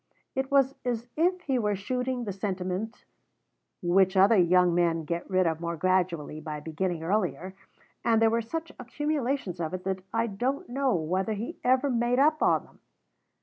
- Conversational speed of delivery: Yes, average, 175 wpm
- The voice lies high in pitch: Yes, high, 200 Hz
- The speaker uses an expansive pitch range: Yes, wide, 5.8 semitones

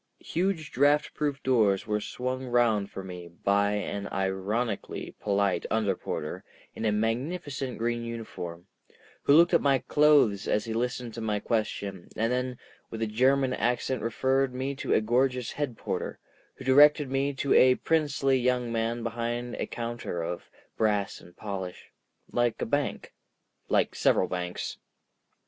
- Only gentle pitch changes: No, average, 4.2 semitones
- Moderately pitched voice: No, low, 120 Hz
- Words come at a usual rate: Yes, average, 150 wpm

